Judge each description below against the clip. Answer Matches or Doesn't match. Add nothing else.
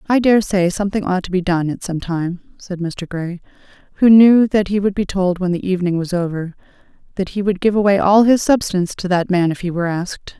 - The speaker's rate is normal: Doesn't match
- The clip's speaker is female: Matches